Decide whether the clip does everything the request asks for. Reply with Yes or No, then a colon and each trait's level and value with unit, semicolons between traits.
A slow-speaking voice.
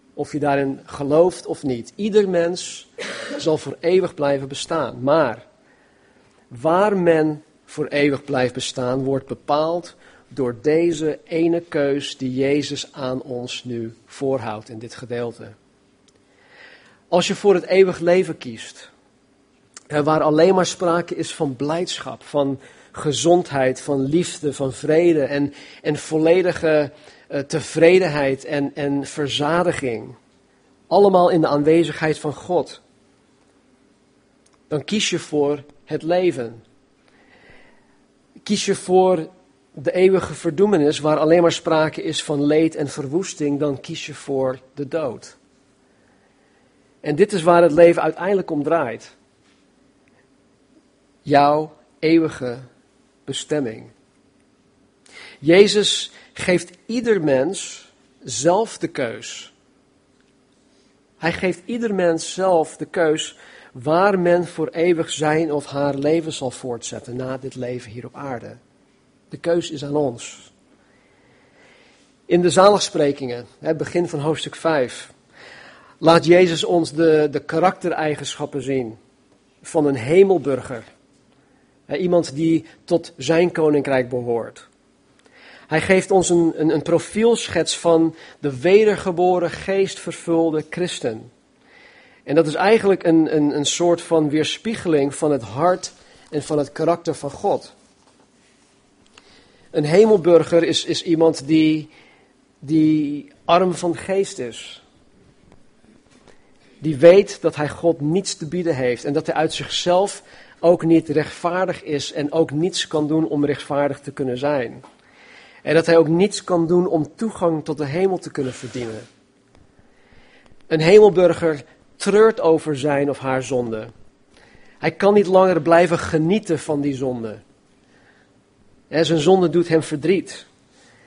Yes: slow, 125 wpm